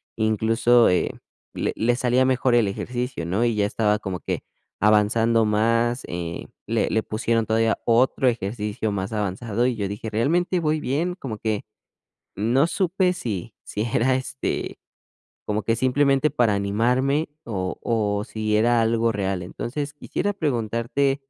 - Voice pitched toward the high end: No, low, 115 Hz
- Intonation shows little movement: No, average, 3.4 semitones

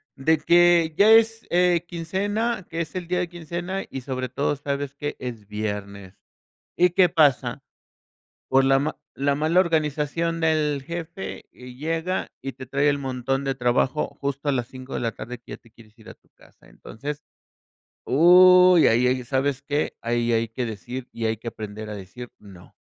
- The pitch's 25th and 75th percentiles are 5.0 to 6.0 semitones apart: Yes, wide, 5.4 semitones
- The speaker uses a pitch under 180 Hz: Yes, medium, 140 Hz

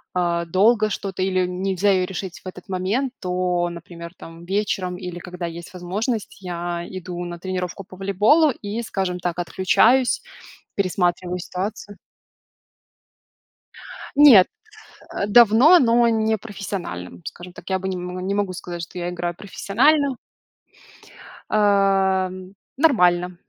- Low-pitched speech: No, medium, 185 Hz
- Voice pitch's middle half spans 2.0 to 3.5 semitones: Yes, narrow, 2.6 semitones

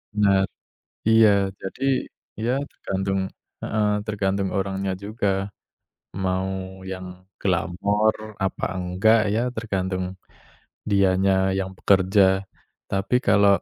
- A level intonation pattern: Yes, narrow, 1.3 semitones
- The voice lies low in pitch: Yes, very low, 95 Hz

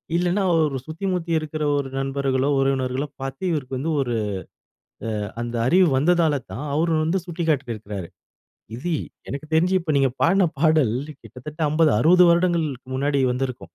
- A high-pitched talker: No, medium, 150 Hz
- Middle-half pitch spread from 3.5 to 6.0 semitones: Yes, average, 3.9 semitones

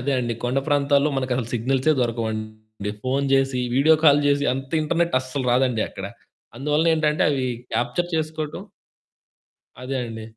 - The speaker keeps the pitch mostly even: No, average, 3.3 semitones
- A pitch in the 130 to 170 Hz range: Yes, low, 135 Hz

